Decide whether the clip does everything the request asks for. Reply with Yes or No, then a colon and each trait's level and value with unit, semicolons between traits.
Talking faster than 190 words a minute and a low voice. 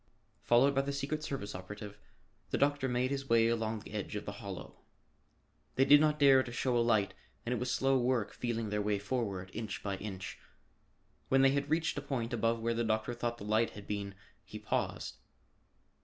Yes: average, 200 wpm; low, 115 Hz